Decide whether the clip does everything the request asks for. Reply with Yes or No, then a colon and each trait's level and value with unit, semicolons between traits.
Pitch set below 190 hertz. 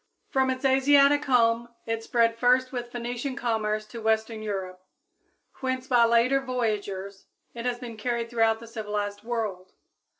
No: high, 235 Hz